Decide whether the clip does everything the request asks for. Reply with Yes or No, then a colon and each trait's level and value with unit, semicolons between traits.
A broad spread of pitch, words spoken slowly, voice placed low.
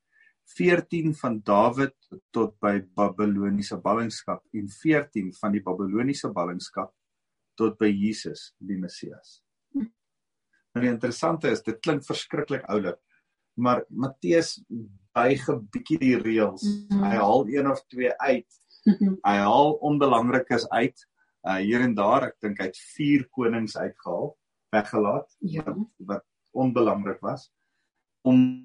Yes: wide, 7.3 semitones; slow, 120 wpm; low, 125 Hz